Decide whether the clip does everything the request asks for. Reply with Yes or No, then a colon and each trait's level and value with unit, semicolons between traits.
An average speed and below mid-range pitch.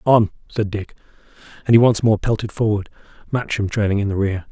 Yes: average, 185 wpm; low, 105 Hz